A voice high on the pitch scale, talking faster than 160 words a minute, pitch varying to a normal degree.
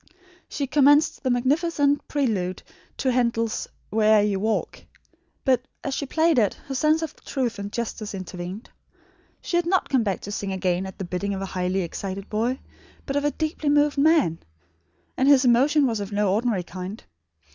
No: high, 235 Hz; average, 180 wpm; wide, 6.4 semitones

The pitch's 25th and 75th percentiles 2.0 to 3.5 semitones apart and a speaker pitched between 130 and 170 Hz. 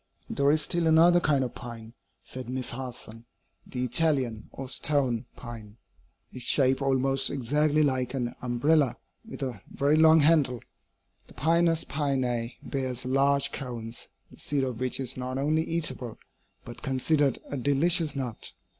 Yes: average, 3.1 semitones; low, 135 Hz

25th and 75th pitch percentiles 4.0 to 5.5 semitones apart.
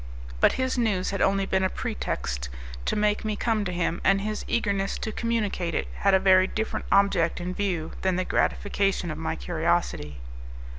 No: average, 3.1 semitones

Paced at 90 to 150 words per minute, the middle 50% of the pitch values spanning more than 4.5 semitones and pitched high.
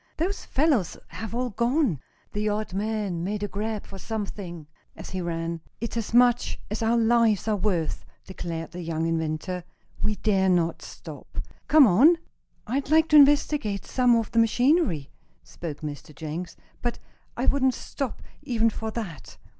No: average, 160 wpm; wide, 5.6 semitones; high, 215 Hz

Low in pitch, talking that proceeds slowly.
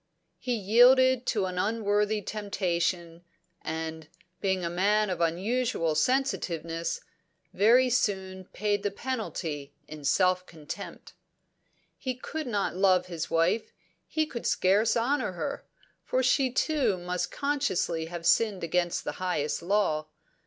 No: high, 195 Hz; slow, 125 wpm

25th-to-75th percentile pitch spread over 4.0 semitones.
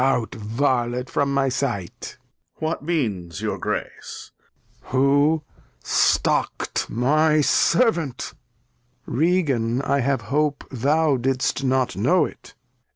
No: average, 3.7 semitones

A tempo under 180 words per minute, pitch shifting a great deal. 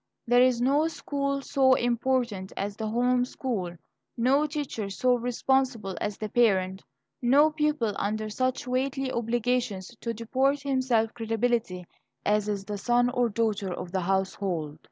No: average, 145 wpm; average, 4.0 semitones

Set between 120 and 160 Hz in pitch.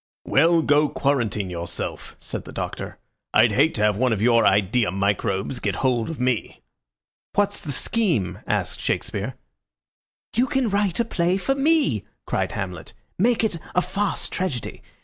Yes: medium, 140 Hz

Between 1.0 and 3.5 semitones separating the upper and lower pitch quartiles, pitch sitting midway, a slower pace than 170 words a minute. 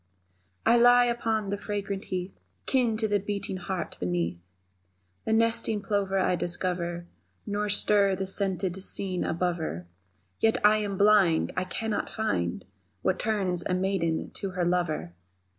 No: average, 2.9 semitones; high, 195 Hz; average, 145 wpm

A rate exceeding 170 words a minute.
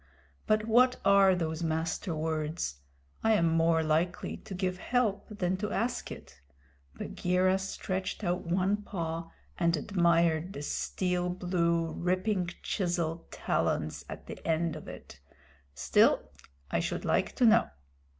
No: slow, 135 wpm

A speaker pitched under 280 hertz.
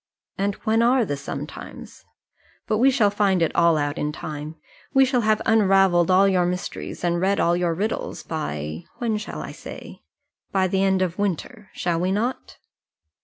Yes: high, 190 Hz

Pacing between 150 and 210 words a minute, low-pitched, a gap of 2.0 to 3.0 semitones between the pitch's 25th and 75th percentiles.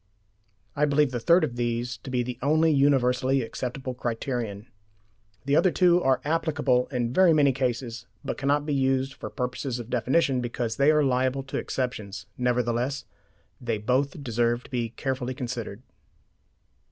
Yes: average, 155 wpm; low, 130 Hz; narrow, 2.6 semitones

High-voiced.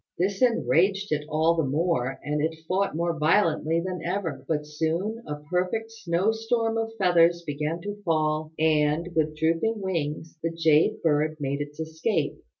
No: medium, 165 Hz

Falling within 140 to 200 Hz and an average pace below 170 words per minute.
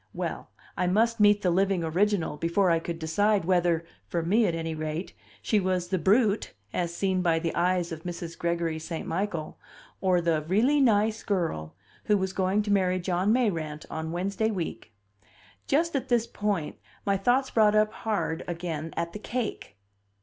No: medium, 185 Hz; average, 175 wpm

